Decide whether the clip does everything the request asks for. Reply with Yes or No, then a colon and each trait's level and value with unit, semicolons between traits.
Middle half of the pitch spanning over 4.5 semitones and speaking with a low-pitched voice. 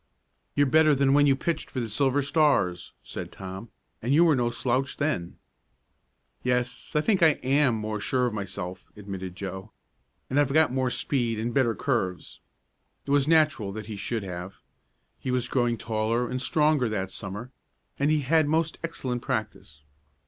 Yes: average, 5.1 semitones; low, 125 Hz